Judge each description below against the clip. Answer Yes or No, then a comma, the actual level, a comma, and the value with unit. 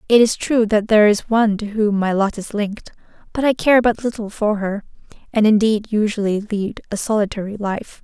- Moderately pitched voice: No, high, 215 Hz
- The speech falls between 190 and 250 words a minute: Yes, average, 200 wpm